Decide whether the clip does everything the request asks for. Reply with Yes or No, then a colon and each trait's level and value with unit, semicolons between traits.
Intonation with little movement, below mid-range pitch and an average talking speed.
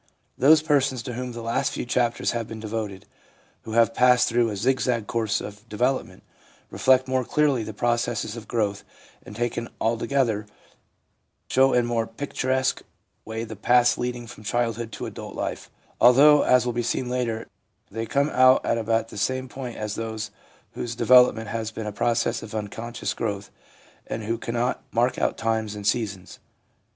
Yes: narrow, 2.1 semitones; low, 115 Hz; average, 175 wpm